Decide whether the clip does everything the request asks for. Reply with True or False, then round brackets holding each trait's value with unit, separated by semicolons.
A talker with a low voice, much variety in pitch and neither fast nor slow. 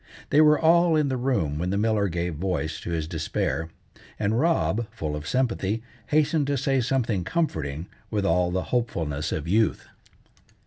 True (105 Hz; 8.4 semitones; 170 wpm)